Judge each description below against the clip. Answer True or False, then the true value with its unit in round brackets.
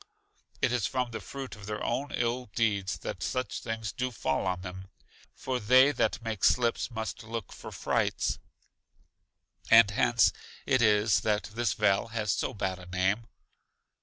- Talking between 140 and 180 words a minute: True (165 wpm)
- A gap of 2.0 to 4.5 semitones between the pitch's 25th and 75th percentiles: True (3.2 semitones)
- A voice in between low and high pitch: False (110 Hz)